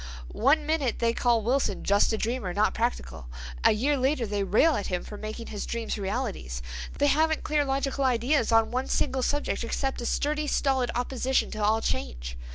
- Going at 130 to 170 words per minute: No, average, 180 wpm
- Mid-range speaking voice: No, high, 240 Hz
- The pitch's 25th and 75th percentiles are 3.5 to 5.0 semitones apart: Yes, average, 4.6 semitones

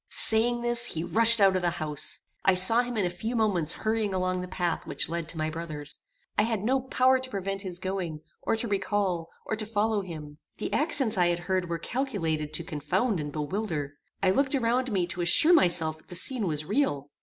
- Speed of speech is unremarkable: No, fast, 215 wpm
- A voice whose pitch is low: No, high, 190 Hz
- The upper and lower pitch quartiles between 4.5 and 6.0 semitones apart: Yes, average, 5.3 semitones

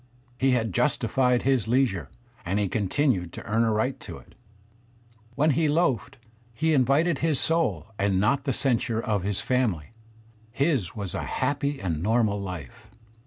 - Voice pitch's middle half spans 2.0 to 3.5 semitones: No, wide, 5.5 semitones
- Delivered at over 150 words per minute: Yes, average, 160 wpm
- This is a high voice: No, low, 120 Hz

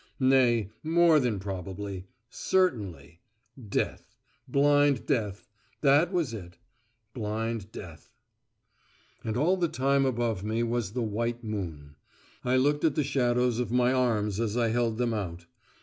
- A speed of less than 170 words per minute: Yes, slow, 135 wpm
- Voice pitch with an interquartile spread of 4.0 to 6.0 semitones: Yes, average, 4.4 semitones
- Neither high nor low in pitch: No, low, 120 Hz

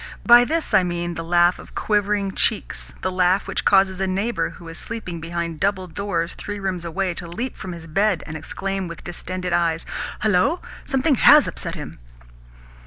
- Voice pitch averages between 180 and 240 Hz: Yes, medium, 185 Hz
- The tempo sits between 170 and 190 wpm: Yes, average, 180 wpm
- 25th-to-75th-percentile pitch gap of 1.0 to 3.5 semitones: Yes, average, 3.1 semitones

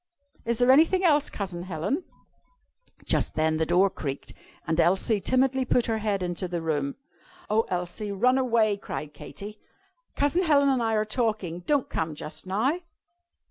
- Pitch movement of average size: No, wide, 6.7 semitones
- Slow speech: No, average, 160 wpm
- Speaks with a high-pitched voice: Yes, high, 210 Hz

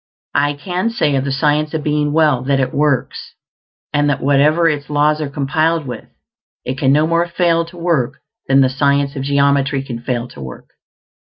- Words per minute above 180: Yes, average, 190 wpm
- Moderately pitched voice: Yes, medium, 145 Hz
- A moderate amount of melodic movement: No, narrow, 2.2 semitones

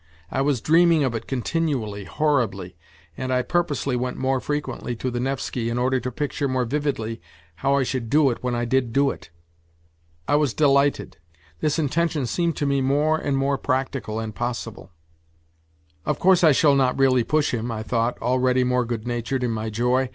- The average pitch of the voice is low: Yes, low, 130 Hz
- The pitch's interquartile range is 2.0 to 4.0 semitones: Yes, average, 3.1 semitones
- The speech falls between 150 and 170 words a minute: No, average, 190 wpm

